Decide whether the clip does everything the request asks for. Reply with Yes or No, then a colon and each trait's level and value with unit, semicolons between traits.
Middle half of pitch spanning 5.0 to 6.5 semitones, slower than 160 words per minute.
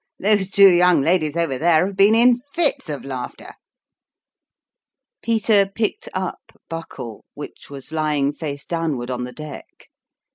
Yes: wide, 5.6 semitones; average, 145 wpm